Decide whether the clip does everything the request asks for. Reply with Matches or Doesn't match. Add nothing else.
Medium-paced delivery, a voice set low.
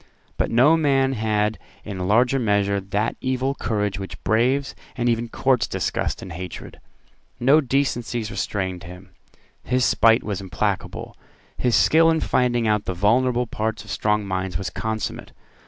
Matches